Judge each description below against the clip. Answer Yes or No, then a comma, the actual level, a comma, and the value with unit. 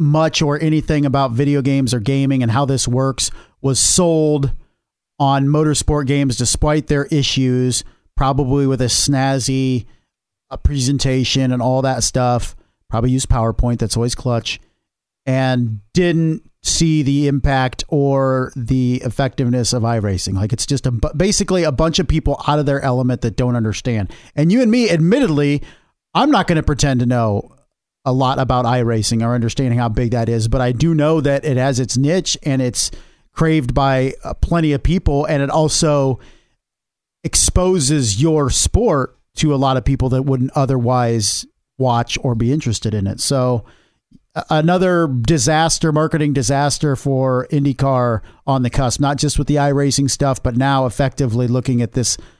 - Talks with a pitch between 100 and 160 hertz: Yes, low, 135 Hz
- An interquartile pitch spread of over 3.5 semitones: No, average, 3.0 semitones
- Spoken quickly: No, average, 160 wpm